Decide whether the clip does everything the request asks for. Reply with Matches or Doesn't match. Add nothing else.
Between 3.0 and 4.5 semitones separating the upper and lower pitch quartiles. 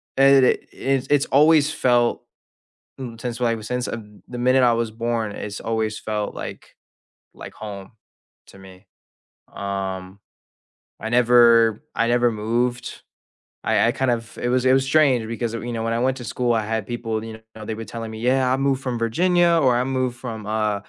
Doesn't match